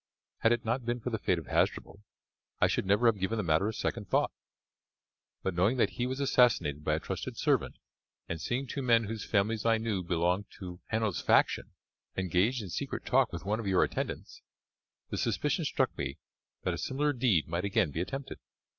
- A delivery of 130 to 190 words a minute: No, average, 200 wpm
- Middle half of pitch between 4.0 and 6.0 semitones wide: Yes, average, 4.8 semitones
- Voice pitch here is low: Yes, low, 105 Hz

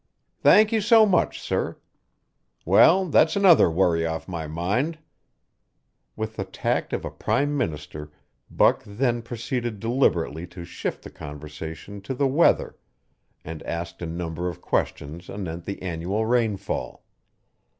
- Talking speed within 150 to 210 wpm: No, slow, 135 wpm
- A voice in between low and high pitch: No, very low, 95 Hz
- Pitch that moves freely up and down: Yes, wide, 7.3 semitones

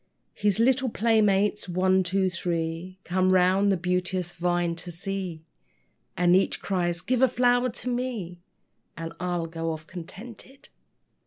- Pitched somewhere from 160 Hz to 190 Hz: Yes, medium, 185 Hz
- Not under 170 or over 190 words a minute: No, average, 140 wpm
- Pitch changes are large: No, average, 3.2 semitones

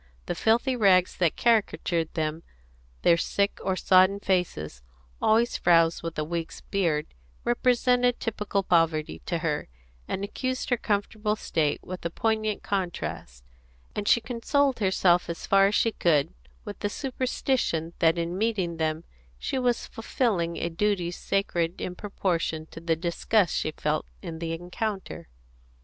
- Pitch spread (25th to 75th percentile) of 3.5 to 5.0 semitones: Yes, average, 4.7 semitones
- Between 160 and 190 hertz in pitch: Yes, medium, 185 Hz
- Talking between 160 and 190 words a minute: No, average, 145 wpm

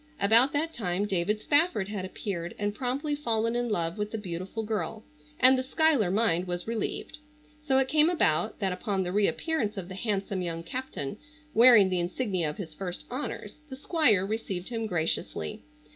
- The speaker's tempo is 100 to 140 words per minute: No, average, 175 wpm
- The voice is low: No, high, 210 Hz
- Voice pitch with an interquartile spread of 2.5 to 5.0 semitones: No, wide, 5.5 semitones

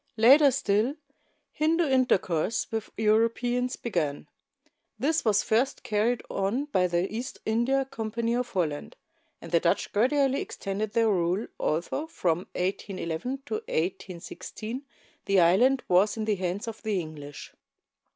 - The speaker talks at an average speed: No, slow, 130 wpm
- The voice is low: No, high, 215 Hz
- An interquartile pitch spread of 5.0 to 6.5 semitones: Yes, wide, 5.4 semitones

